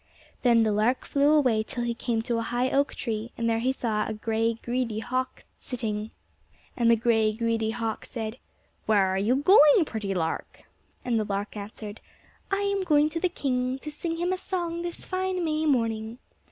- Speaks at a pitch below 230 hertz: No, high, 235 Hz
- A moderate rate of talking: Yes, average, 195 wpm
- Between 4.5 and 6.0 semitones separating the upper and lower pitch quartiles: Yes, average, 4.9 semitones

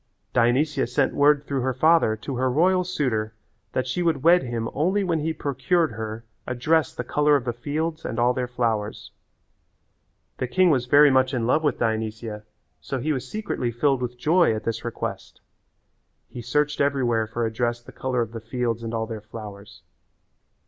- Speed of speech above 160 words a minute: Yes, average, 190 wpm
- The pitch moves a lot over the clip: No, average, 4.3 semitones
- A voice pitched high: No, low, 125 Hz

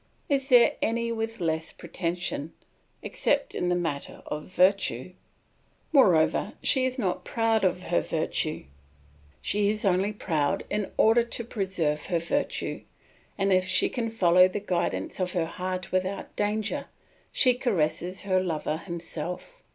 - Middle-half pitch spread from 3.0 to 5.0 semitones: Yes, average, 4.6 semitones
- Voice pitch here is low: No, medium, 185 Hz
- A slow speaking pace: No, average, 145 wpm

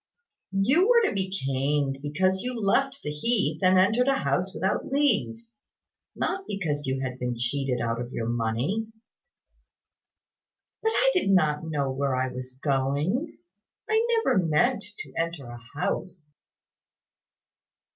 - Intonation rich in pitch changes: Yes, wide, 8.9 semitones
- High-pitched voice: No, medium, 160 Hz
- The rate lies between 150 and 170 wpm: No, slow, 135 wpm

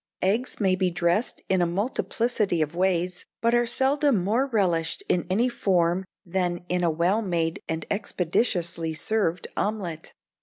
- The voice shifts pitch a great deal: No, average, 4.1 semitones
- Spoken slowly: No, average, 150 wpm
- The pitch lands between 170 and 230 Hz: Yes, medium, 185 Hz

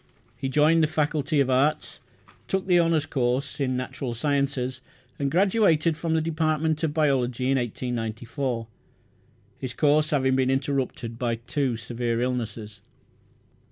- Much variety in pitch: No, average, 3.8 semitones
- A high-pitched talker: No, low, 135 Hz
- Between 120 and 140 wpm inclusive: Yes, slow, 135 wpm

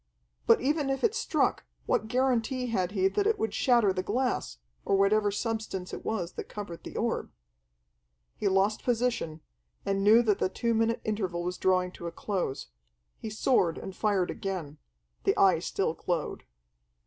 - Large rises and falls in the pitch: No, average, 4.0 semitones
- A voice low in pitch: No, high, 205 Hz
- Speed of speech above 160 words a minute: Yes, average, 170 wpm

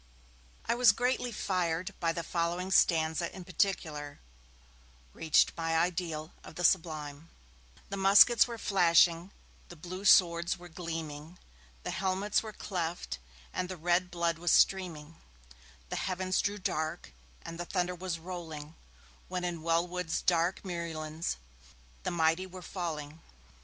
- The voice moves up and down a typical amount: No, narrow, 2.2 semitones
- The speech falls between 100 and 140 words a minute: Yes, slow, 135 wpm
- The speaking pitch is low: No, medium, 175 Hz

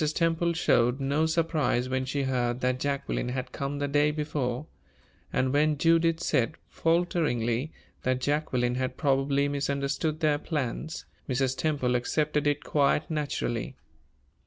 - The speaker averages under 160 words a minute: Yes, slow, 135 wpm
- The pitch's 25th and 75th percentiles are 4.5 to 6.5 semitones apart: No, average, 3.1 semitones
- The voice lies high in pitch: No, medium, 140 Hz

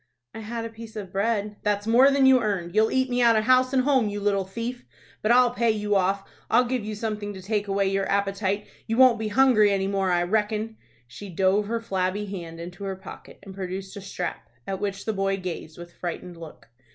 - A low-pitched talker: No, high, 205 Hz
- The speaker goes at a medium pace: No, fast, 225 wpm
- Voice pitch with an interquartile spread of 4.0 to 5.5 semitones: No, average, 2.9 semitones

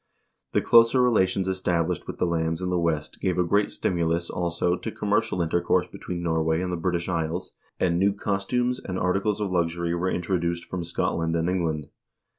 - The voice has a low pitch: Yes, very low, 90 Hz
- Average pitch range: No, narrow, 2.0 semitones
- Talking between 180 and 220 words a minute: Yes, average, 185 wpm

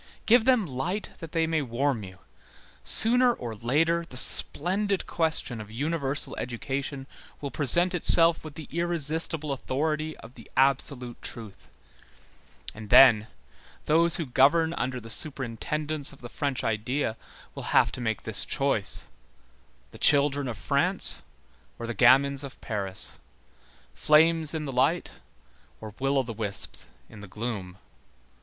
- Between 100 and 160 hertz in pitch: Yes, medium, 140 Hz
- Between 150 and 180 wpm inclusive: No, average, 140 wpm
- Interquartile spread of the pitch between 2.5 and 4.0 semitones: No, average, 5.3 semitones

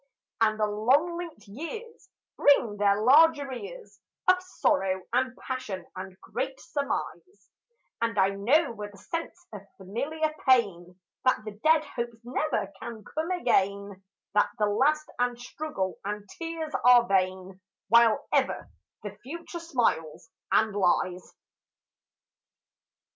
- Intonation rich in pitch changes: Yes, wide, 7.4 semitones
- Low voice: No, high, 235 Hz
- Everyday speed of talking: No, slow, 125 wpm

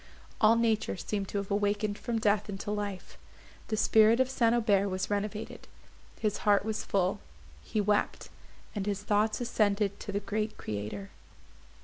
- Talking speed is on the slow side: No, average, 155 wpm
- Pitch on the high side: Yes, high, 205 Hz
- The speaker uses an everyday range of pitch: No, narrow, 1.4 semitones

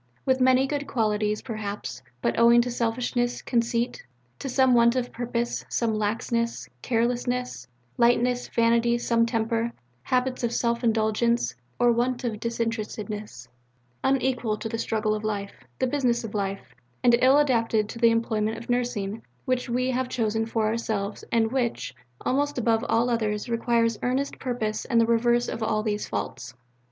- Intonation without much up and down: Yes, narrow, 2.0 semitones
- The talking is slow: No, average, 155 wpm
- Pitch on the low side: No, high, 235 Hz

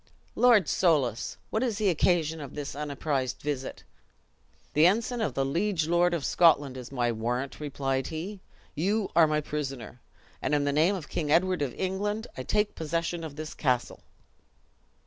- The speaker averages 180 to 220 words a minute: No, average, 165 wpm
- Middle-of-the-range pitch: Yes, medium, 155 Hz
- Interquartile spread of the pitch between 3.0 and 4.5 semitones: No, average, 5.0 semitones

